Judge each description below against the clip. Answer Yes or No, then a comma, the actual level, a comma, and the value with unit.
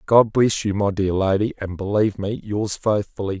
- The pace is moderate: Yes, average, 195 wpm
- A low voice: Yes, low, 100 Hz